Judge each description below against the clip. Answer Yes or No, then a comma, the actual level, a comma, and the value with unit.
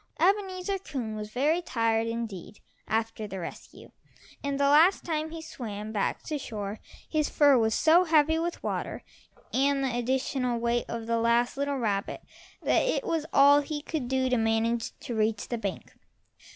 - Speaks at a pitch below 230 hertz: No, very high, 255 Hz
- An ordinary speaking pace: Yes, average, 170 wpm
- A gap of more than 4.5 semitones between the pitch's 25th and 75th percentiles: Yes, average, 5.3 semitones